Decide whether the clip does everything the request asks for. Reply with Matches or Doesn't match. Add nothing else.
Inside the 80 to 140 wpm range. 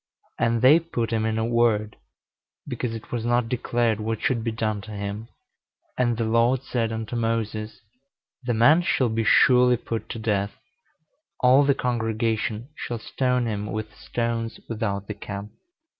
Doesn't match